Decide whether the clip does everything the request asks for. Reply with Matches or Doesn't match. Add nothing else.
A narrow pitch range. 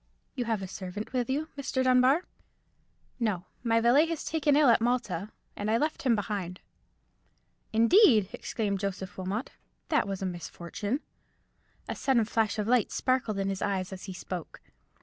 Doesn't match